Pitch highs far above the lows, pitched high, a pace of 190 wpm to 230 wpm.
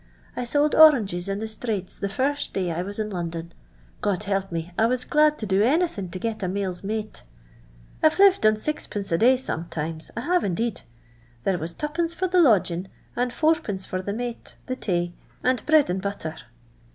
Yes: wide, 5.9 semitones; high, 210 Hz; average, 200 wpm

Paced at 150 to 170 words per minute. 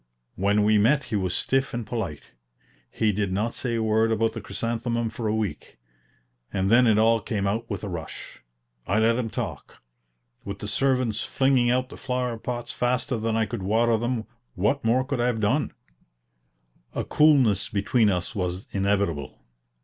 No: average, 180 wpm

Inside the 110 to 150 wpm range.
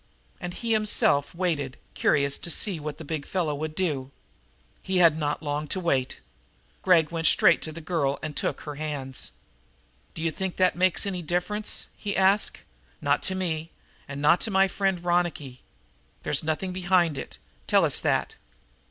No: average, 170 wpm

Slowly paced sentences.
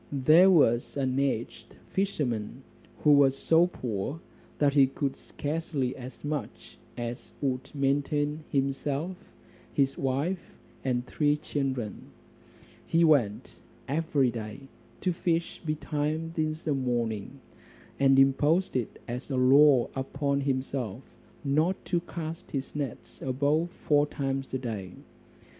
Yes: slow, 120 wpm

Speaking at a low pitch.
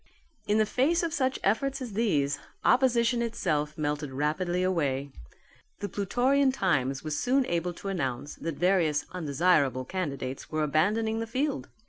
No: medium, 185 Hz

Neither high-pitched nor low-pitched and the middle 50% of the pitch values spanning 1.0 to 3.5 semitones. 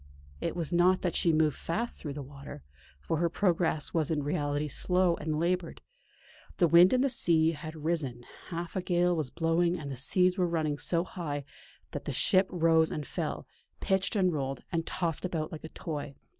Yes: medium, 165 Hz; average, 2.9 semitones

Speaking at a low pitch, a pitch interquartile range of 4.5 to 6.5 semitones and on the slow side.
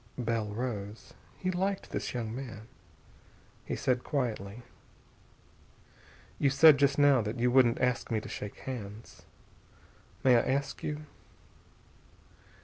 No: low, 125 Hz; average, 3.7 semitones; slow, 120 wpm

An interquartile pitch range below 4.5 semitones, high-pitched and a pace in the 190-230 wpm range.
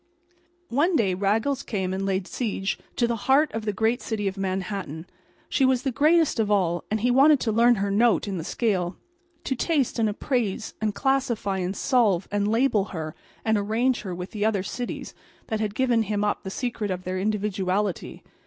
Yes: average, 3.9 semitones; high, 215 Hz; average, 195 wpm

